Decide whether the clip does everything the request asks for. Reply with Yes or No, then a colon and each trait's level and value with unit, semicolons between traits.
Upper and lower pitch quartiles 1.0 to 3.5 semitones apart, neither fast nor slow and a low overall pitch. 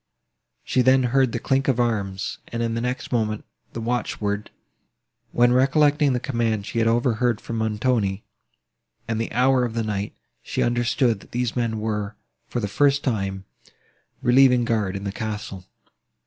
Yes: average, 2.7 semitones; average, 165 wpm; low, 115 Hz